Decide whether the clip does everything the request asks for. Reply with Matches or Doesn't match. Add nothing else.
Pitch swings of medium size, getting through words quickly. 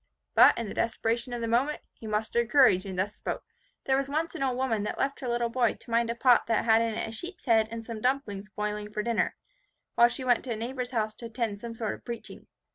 Doesn't match